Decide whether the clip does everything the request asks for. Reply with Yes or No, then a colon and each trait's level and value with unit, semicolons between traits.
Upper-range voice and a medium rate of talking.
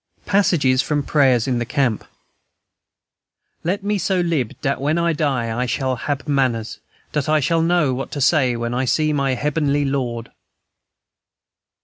No: medium, 140 Hz; average, 155 wpm